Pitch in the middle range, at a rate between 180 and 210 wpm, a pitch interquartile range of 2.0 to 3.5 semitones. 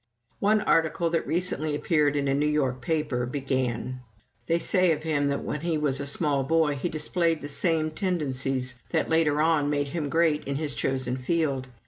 Yes: medium, 150 Hz; average, 185 wpm; average, 3.0 semitones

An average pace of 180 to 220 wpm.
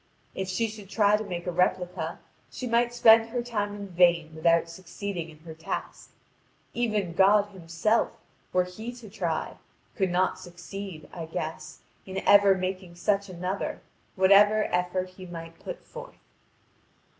No: average, 150 wpm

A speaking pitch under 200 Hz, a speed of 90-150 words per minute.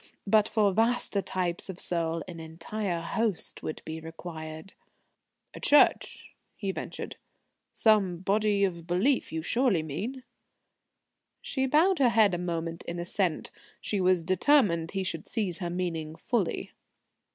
Yes: medium, 185 Hz; average, 140 wpm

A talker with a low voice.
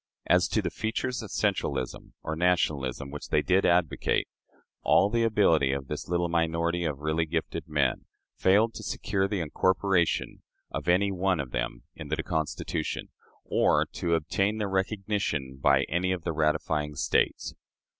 Yes: very low, 85 Hz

